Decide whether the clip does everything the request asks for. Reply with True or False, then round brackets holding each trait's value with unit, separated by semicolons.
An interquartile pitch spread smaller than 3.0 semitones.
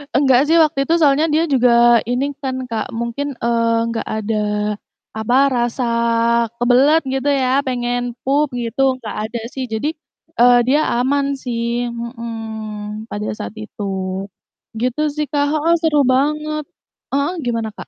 False (3.3 semitones)